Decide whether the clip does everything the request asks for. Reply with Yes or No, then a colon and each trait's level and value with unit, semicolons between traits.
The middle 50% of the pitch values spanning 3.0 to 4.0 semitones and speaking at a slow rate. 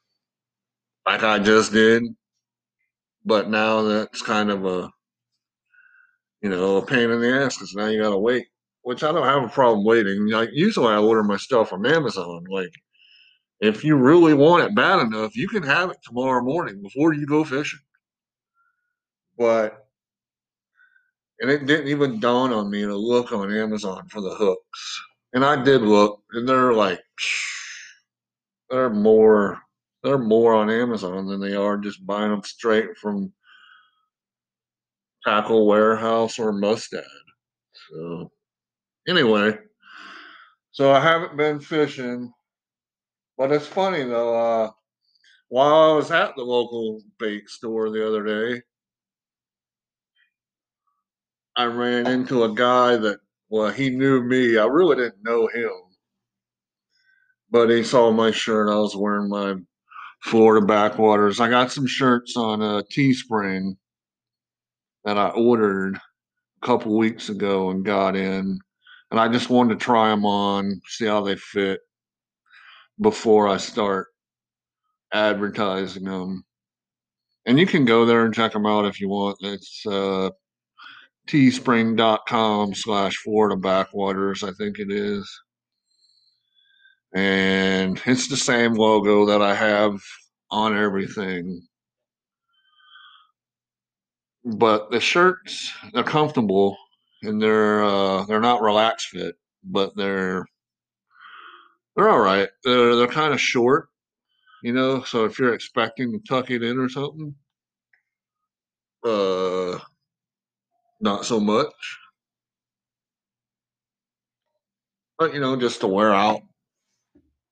No: average, 4.6 semitones; slow, 130 wpm